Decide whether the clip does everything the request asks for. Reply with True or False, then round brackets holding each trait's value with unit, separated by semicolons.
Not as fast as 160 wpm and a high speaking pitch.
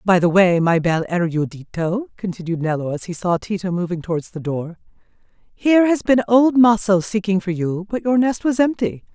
False (190 wpm; 195 Hz)